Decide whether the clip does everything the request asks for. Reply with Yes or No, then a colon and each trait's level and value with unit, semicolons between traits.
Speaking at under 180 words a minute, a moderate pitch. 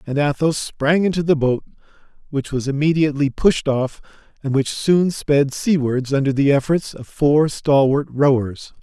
Yes: average, 155 wpm; medium, 145 Hz